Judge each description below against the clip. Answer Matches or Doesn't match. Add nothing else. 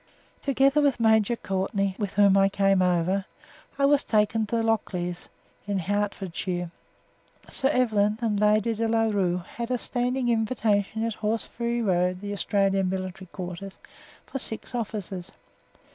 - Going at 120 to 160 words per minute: Matches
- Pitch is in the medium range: Doesn't match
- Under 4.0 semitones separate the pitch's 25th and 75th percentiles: Matches